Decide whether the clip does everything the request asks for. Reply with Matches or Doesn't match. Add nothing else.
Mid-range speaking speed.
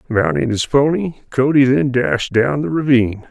Matches